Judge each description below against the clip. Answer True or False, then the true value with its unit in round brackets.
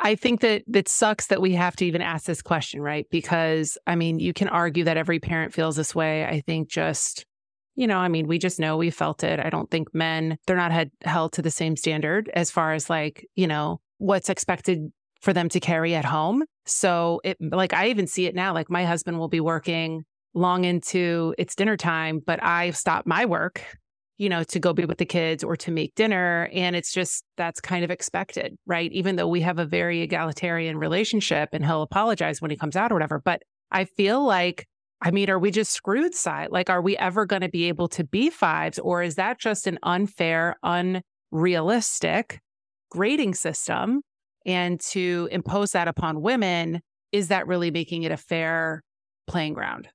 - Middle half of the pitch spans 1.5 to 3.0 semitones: True (2.5 semitones)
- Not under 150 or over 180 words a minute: False (205 wpm)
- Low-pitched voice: False (175 Hz)